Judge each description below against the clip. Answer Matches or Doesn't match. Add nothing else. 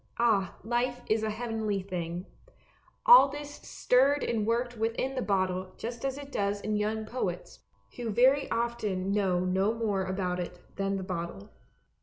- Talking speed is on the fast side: Doesn't match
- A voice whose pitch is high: Matches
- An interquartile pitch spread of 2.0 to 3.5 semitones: Doesn't match